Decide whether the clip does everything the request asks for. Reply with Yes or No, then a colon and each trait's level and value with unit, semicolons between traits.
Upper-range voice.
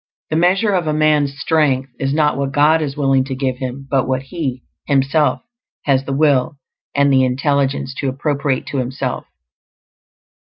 No: medium, 140 Hz